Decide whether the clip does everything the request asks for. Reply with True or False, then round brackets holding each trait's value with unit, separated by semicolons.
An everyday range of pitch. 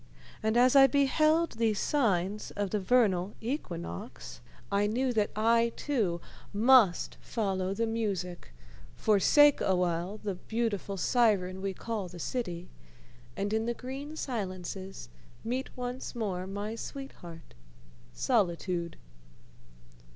True (4.7 semitones)